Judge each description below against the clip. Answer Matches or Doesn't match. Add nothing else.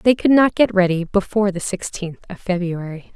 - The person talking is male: Doesn't match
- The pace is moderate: Matches